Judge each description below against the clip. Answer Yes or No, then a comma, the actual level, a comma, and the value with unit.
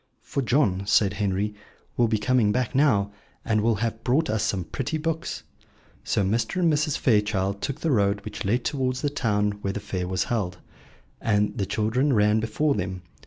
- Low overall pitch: Yes, low, 110 Hz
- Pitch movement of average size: Yes, average, 4.3 semitones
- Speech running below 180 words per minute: No, average, 185 wpm